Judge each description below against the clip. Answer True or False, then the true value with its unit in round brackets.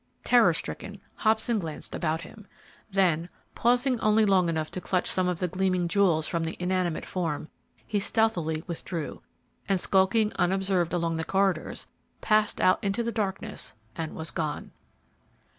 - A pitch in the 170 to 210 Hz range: True (185 Hz)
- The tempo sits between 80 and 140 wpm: False (150 wpm)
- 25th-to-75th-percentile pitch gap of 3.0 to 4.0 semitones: True (3.6 semitones)